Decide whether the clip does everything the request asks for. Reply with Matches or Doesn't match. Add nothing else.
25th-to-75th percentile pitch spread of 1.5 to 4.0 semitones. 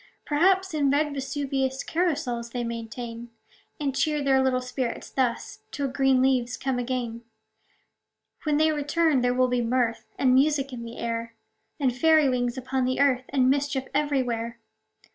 Matches